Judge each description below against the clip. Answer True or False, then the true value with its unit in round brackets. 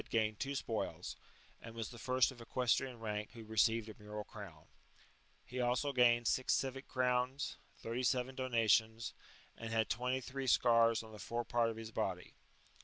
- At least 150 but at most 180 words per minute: True (175 wpm)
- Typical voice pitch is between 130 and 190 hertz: False (115 Hz)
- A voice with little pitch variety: True (2.3 semitones)